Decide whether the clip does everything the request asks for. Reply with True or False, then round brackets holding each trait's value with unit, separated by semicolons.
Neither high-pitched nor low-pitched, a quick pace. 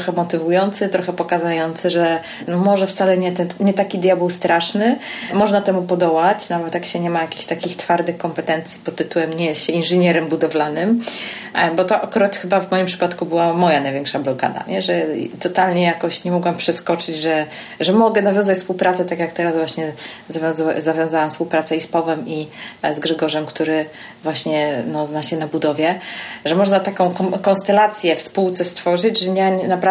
True (170 Hz; 175 wpm)